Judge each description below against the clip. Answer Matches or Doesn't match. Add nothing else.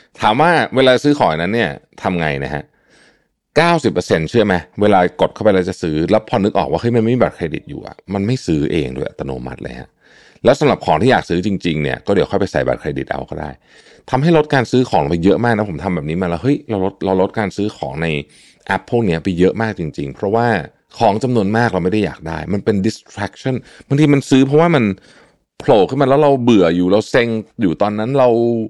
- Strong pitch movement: Matches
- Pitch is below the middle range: Matches